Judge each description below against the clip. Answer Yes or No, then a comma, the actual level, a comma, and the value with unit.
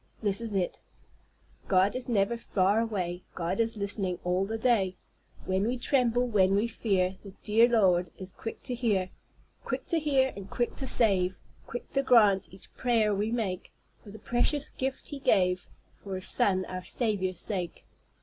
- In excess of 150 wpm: Yes, average, 175 wpm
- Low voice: No, high, 205 Hz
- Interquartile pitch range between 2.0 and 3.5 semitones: No, average, 4.0 semitones